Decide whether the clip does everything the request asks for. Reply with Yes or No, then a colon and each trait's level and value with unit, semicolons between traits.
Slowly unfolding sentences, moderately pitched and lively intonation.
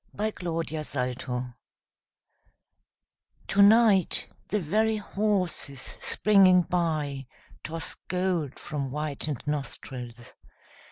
Yes: slow, 75 wpm; medium, 160 Hz; wide, 5.8 semitones